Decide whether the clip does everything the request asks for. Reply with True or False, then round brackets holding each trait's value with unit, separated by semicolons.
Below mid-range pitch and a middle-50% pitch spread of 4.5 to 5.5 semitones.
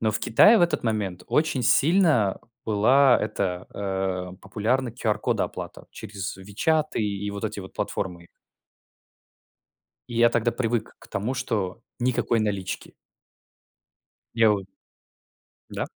False (110 Hz; 3.8 semitones)